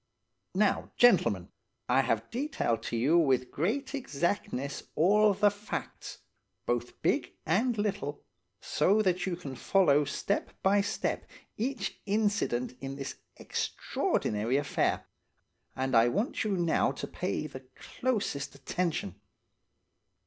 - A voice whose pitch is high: No, medium, 170 Hz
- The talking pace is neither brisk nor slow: No, slow, 120 wpm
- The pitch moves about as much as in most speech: No, wide, 7.6 semitones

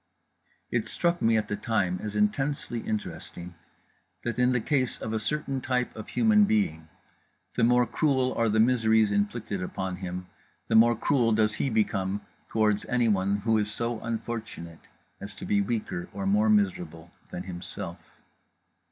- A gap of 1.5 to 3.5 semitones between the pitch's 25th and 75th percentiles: Yes, average, 3.2 semitones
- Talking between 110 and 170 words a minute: Yes, average, 160 wpm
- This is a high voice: No, low, 110 Hz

